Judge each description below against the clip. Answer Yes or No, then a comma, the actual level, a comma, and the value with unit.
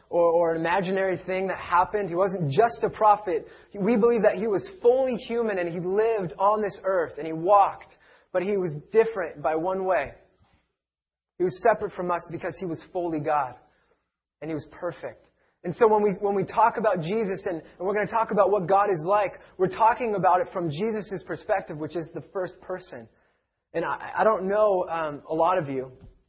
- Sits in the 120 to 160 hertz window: No, high, 190 Hz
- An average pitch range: Yes, average, 3.6 semitones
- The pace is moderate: No, fast, 210 wpm